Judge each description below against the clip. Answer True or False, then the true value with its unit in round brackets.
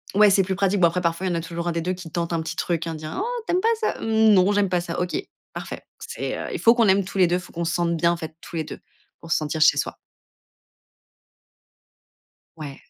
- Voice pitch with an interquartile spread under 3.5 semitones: True (2.9 semitones)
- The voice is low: False (175 Hz)